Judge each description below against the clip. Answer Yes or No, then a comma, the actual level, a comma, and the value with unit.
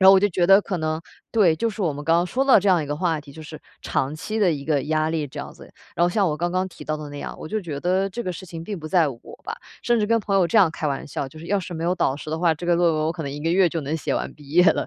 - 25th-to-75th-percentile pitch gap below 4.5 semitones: Yes, average, 3.5 semitones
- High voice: No, medium, 165 Hz